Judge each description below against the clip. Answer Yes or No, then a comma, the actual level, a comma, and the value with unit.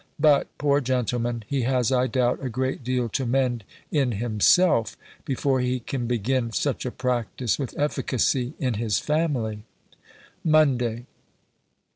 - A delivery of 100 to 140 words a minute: Yes, slow, 135 wpm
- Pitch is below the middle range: Yes, low, 125 Hz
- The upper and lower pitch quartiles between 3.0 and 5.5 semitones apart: No, narrow, 2.4 semitones